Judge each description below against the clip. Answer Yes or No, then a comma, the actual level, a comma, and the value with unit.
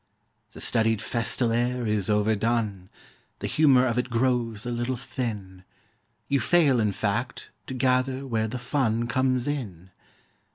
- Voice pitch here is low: Yes, low, 120 Hz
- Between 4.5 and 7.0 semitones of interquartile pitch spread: No, average, 2.7 semitones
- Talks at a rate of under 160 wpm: Yes, average, 140 wpm